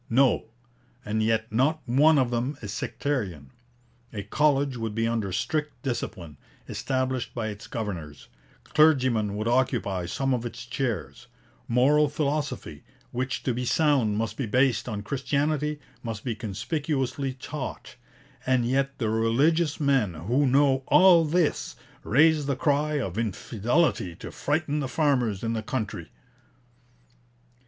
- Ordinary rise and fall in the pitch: Yes, average, 4.5 semitones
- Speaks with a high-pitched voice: No, low, 130 Hz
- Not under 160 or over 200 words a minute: No, slow, 135 wpm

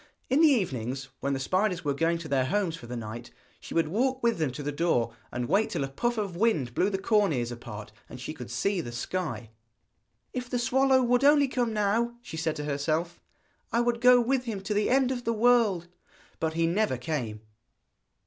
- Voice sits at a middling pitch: Yes, medium, 175 Hz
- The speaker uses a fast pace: Yes, fast, 215 wpm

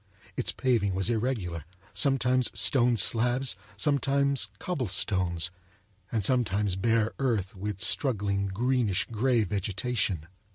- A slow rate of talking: Yes, slow, 100 wpm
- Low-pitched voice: Yes, low, 110 Hz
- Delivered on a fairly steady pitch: No, average, 4.6 semitones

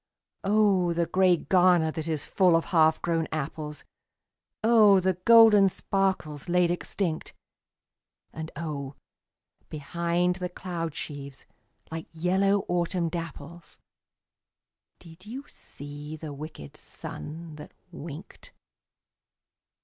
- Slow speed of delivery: Yes, slow, 105 wpm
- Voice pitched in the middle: Yes, medium, 170 Hz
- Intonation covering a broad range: No, average, 2.9 semitones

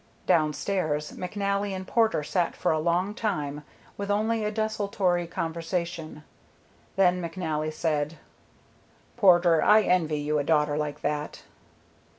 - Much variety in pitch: No, average, 4.5 semitones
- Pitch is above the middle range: No, medium, 175 Hz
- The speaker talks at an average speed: No, slow, 125 wpm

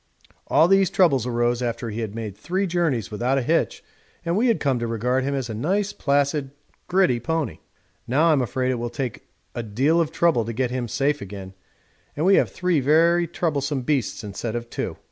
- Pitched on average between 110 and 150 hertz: Yes, low, 135 Hz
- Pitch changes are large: Yes, wide, 5.7 semitones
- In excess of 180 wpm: Yes, average, 200 wpm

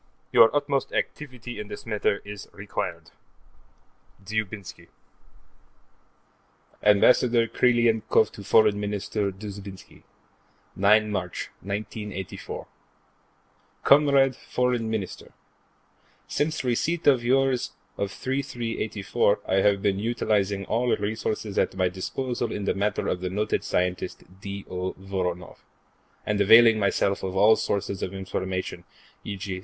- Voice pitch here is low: Yes, low, 105 Hz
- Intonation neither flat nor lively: Yes, average, 3.3 semitones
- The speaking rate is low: Yes, slow, 110 wpm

